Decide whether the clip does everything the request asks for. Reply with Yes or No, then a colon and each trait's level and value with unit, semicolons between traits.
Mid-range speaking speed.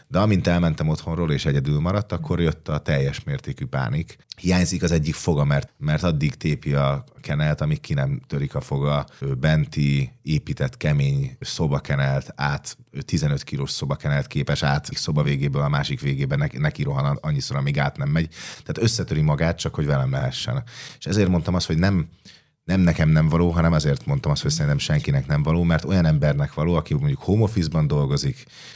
No: fast, 175 wpm